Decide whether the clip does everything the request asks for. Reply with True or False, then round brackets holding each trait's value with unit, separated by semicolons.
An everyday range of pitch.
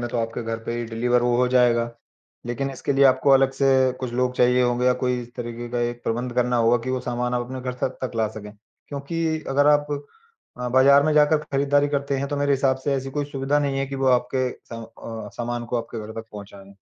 False (2.3 semitones)